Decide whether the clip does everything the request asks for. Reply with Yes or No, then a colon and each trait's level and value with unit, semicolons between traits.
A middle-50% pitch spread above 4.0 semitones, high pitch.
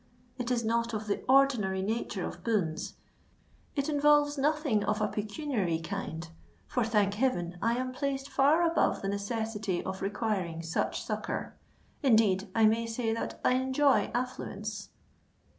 Yes: average, 4.6 semitones; high, 225 Hz